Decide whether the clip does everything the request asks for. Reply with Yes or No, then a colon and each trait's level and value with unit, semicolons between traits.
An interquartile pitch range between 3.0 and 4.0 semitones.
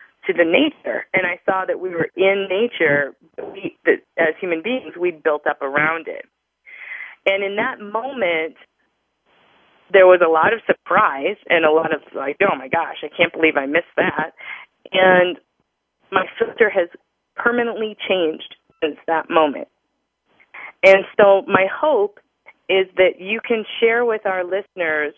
No: wide, 5.4 semitones